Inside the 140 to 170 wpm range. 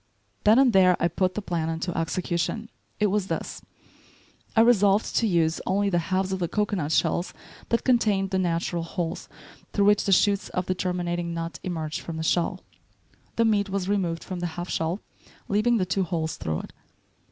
No: average, 185 wpm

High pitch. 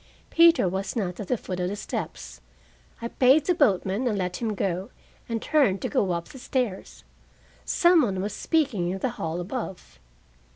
Yes: high, 205 Hz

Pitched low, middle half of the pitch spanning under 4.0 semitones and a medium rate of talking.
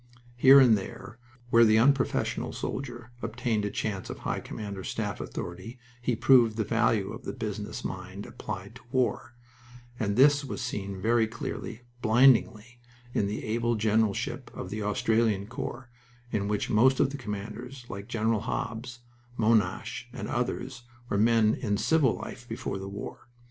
Yes: low, 115 Hz; average, 2.7 semitones; average, 160 wpm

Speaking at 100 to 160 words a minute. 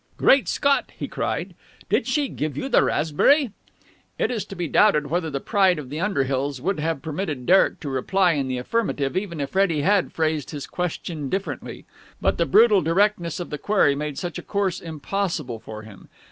No: average, 190 wpm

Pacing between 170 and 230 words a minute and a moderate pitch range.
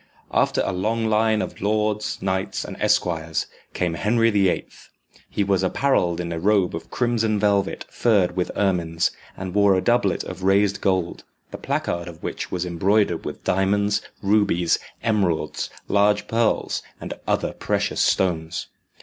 No: average, 150 wpm; average, 3.1 semitones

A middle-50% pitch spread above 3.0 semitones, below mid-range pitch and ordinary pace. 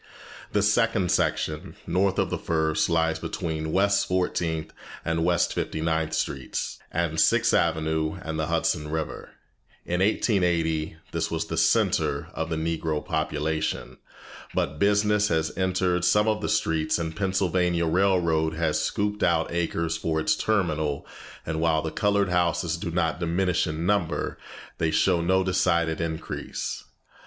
No: narrow, 2.6 semitones; very low, 85 Hz; average, 145 wpm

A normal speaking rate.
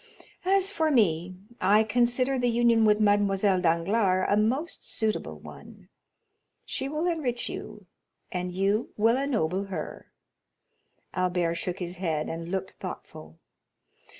No: slow, 125 wpm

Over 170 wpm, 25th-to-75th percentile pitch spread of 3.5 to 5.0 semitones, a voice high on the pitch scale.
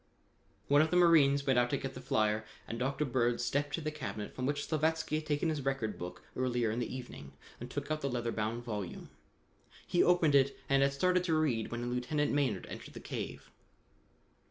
No: fast, 205 wpm; average, 4.2 semitones; low, 135 Hz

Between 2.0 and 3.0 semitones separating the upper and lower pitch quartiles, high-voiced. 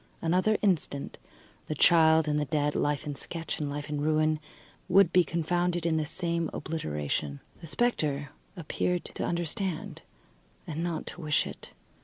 No: average, 2.7 semitones; medium, 160 Hz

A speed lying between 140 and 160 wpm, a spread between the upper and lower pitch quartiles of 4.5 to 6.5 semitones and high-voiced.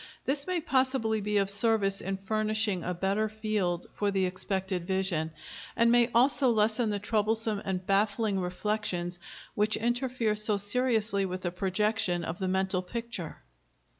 No: average, 150 wpm; average, 2.8 semitones; high, 210 Hz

